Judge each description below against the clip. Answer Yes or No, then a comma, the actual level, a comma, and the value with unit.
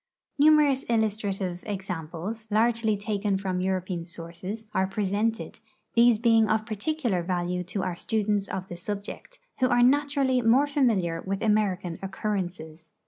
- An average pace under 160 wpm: Yes, average, 140 wpm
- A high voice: Yes, high, 205 Hz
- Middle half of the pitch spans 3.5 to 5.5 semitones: Yes, average, 3.8 semitones